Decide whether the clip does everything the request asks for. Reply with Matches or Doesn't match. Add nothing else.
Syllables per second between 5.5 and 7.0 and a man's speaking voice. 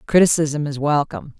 Doesn't match